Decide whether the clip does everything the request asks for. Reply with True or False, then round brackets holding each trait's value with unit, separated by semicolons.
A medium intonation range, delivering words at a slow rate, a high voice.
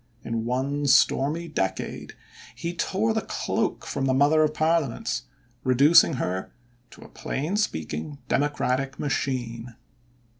False (4.0 semitones; 120 wpm; 140 Hz)